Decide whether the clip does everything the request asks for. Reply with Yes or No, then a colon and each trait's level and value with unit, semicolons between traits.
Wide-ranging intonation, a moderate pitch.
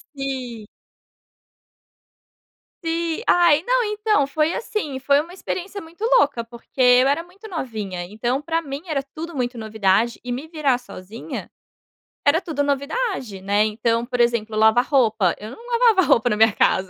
No: wide, 6.4 semitones; very high, 270 Hz